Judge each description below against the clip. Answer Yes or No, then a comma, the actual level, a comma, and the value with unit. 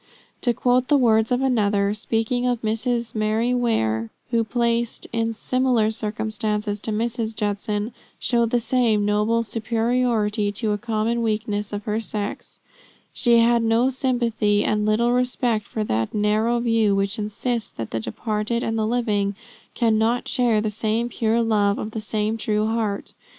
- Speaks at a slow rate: No, average, 155 wpm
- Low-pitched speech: No, high, 220 Hz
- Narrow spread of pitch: Yes, narrow, 2.0 semitones